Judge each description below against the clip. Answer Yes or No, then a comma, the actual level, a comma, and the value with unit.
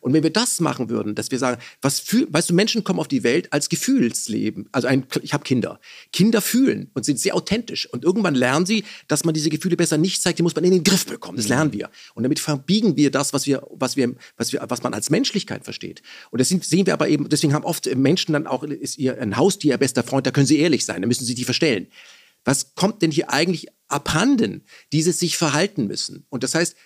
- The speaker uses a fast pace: Yes, fast, 245 wpm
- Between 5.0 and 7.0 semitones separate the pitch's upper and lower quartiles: Yes, wide, 5.4 semitones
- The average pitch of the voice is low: No, medium, 155 Hz